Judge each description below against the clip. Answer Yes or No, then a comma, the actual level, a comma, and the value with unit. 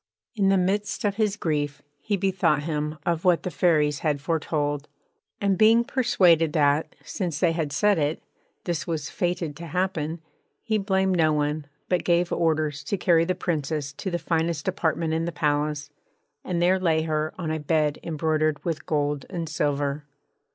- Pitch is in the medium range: Yes, medium, 165 Hz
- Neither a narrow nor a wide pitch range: Yes, average, 3.3 semitones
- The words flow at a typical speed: Yes, average, 170 wpm